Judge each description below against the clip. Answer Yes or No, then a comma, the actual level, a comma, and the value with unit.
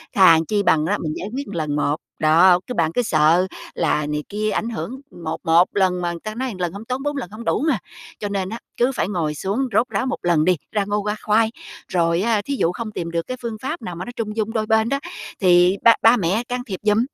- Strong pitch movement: No, average, 4.9 semitones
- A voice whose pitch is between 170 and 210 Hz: Yes, high, 200 Hz